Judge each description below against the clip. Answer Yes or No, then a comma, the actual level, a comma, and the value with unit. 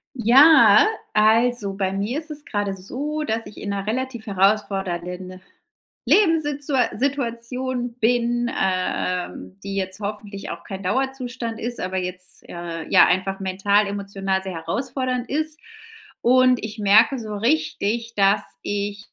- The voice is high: Yes, high, 215 Hz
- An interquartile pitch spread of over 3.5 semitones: Yes, average, 4.5 semitones